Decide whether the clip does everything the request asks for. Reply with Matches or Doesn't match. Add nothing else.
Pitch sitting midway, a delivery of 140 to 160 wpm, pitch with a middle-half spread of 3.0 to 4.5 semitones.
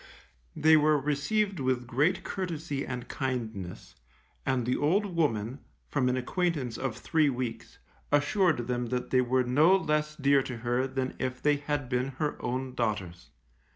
Doesn't match